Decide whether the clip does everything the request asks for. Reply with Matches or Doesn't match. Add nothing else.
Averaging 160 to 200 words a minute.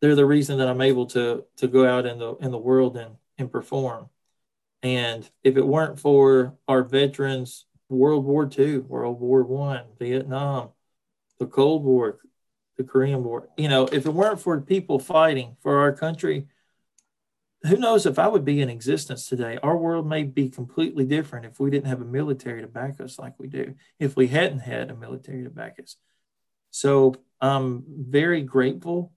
Matches